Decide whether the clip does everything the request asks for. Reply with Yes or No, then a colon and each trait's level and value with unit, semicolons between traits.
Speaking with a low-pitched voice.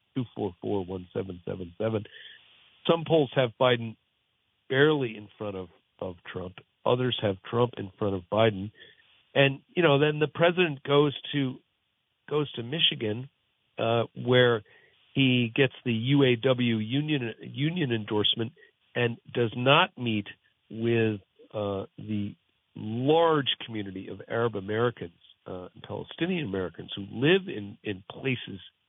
Yes: low, 115 Hz